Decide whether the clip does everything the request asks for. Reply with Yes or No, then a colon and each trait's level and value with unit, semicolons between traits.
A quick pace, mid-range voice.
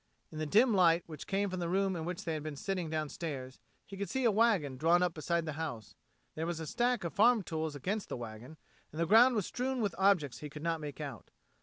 Yes: fast, 250 wpm; medium, 170 Hz